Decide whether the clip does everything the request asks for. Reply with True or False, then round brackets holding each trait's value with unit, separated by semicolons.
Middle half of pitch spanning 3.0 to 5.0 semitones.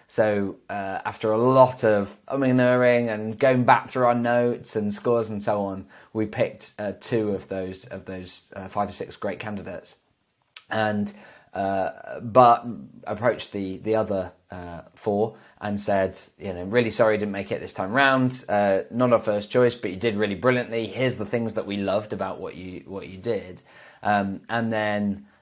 True (3.5 semitones)